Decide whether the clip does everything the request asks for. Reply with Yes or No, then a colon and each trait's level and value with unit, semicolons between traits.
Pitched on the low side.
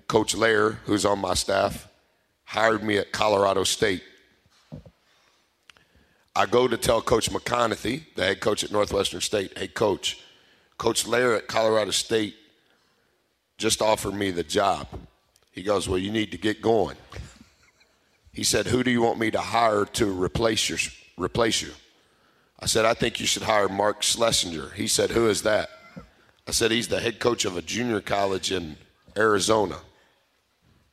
Yes: low, 105 Hz